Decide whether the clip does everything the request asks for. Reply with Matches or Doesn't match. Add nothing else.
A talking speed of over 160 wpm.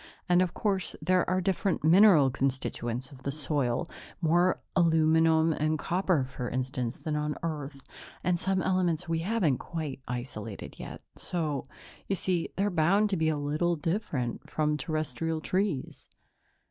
Doesn't match